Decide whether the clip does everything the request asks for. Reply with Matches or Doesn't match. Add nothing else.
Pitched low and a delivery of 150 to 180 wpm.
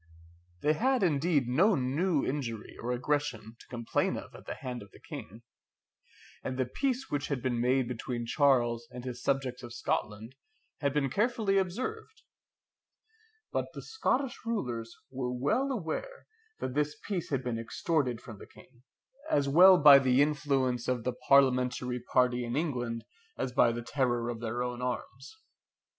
Matches